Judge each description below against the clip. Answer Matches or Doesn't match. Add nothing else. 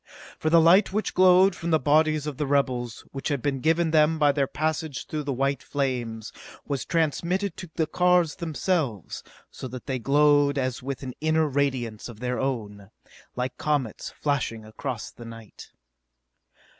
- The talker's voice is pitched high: Doesn't match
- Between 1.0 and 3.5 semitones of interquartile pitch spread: Doesn't match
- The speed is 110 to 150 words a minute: Doesn't match